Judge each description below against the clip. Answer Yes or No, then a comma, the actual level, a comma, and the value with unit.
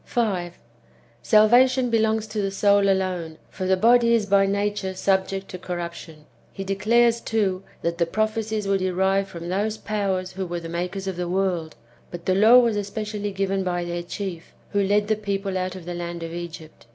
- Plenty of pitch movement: No, average, 2.9 semitones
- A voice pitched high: Yes, high, 195 Hz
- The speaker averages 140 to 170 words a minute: No, average, 190 wpm